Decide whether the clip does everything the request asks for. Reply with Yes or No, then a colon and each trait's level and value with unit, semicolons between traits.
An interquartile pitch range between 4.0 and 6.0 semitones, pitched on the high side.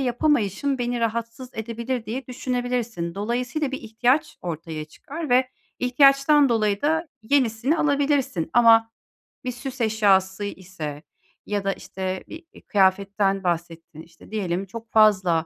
Yes: average, 4.9 semitones; high, 225 Hz